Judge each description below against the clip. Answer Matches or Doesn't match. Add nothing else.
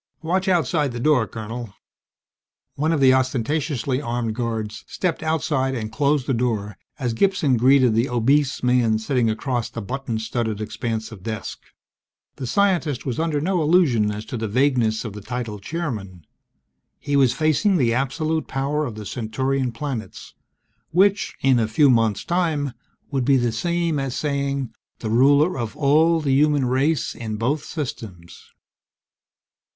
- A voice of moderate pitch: Doesn't match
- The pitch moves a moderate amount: Matches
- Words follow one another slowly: Doesn't match